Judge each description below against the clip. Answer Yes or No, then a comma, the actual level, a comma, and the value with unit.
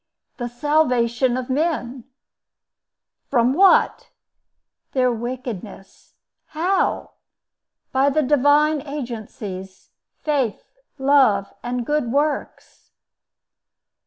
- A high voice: Yes, very high, 260 Hz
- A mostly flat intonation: No, average, 3.6 semitones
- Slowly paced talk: Yes, slow, 75 wpm